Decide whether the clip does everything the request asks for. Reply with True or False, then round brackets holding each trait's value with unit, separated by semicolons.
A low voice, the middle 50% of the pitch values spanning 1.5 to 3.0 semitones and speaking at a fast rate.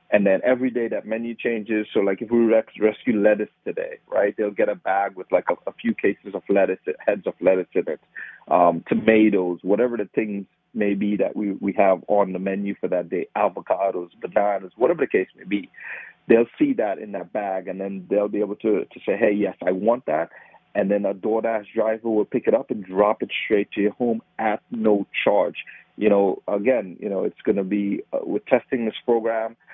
True (105 Hz; 2.5 semitones; 220 wpm)